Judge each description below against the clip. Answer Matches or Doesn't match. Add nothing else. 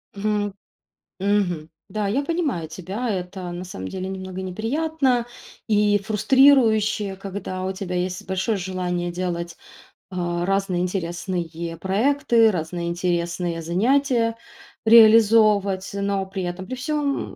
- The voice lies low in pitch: Doesn't match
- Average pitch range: Matches